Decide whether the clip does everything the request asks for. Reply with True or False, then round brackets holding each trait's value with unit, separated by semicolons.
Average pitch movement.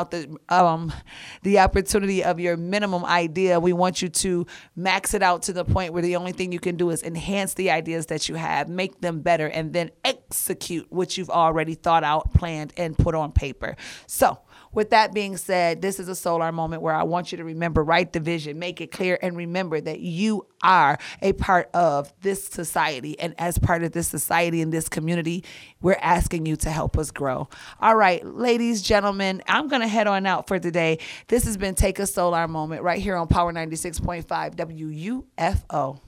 False (2.3 semitones)